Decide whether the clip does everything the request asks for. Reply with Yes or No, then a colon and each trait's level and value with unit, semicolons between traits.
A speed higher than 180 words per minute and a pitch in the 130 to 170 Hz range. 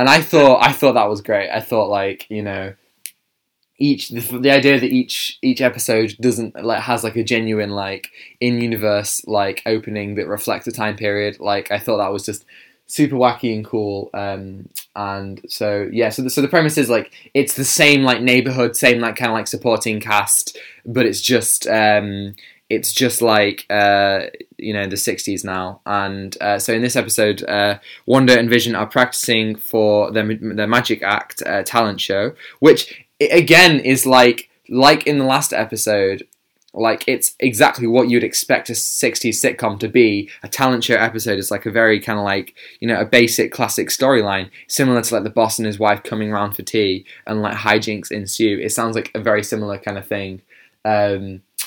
No: average, 195 wpm; low, 110 Hz